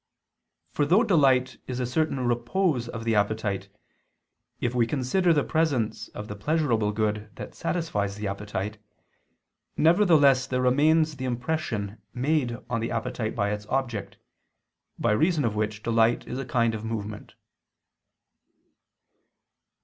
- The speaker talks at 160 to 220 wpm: No, slow, 135 wpm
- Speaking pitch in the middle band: No, low, 120 Hz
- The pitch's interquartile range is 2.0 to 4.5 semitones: No, average, 5.2 semitones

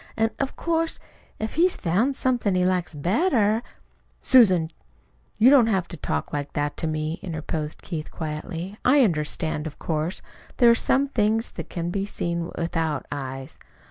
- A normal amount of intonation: No, wide, 6.5 semitones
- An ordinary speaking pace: Yes, average, 165 wpm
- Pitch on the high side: No, medium, 180 Hz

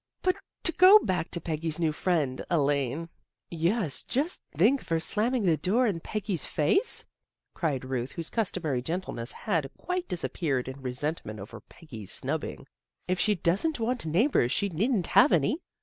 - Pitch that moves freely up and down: Yes, wide, 6.7 semitones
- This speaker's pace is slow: No, average, 180 wpm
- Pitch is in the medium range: Yes, medium, 170 Hz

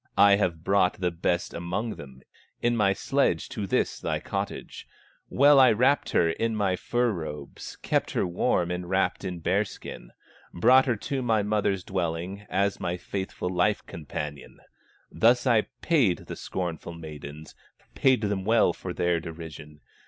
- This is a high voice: No, very low, 95 Hz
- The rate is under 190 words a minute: Yes, average, 155 wpm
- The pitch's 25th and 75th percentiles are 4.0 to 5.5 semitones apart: Yes, average, 4.4 semitones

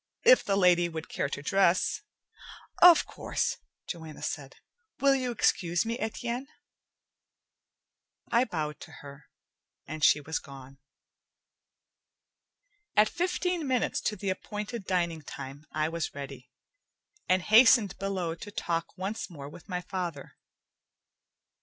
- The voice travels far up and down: Yes, wide, 6.1 semitones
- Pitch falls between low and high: Yes, medium, 180 Hz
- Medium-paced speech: No, slow, 130 wpm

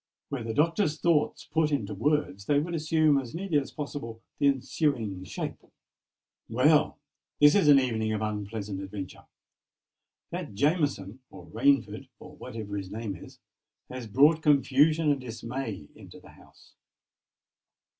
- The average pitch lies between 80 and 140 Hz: Yes, low, 135 Hz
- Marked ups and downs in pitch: Yes, wide, 5.7 semitones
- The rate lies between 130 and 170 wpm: Yes, average, 140 wpm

